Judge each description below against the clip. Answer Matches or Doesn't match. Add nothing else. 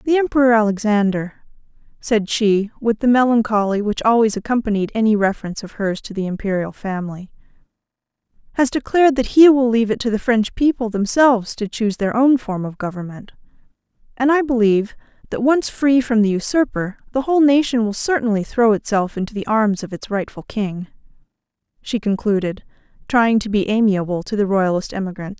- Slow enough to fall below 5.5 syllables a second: Doesn't match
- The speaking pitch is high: Matches